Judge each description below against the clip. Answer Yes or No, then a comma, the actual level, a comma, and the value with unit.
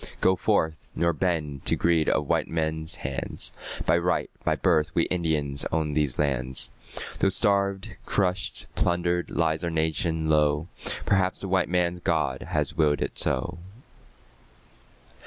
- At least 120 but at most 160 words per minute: Yes, average, 140 wpm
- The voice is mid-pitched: No, very low, 80 Hz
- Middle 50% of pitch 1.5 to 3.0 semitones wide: Yes, narrow, 2.6 semitones